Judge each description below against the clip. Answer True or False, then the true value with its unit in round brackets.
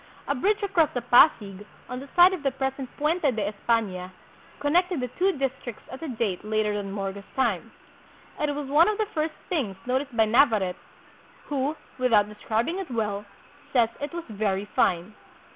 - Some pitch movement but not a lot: False (6.1 semitones)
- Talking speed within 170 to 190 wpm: True (175 wpm)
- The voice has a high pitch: True (250 Hz)